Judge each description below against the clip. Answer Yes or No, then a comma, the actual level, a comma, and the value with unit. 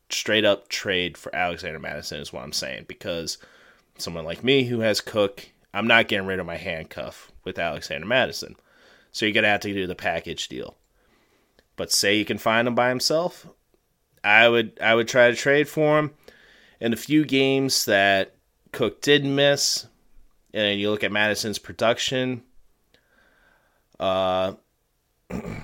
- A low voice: Yes, low, 115 Hz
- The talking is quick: No, average, 160 wpm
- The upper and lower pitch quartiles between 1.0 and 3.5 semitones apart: No, average, 5.2 semitones